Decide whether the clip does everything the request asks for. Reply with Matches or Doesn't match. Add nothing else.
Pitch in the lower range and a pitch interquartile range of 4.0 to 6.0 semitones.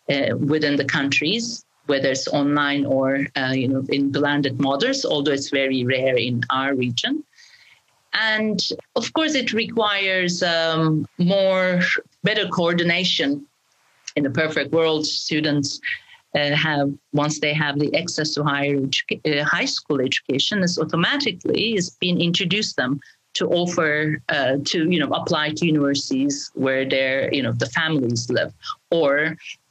Doesn't match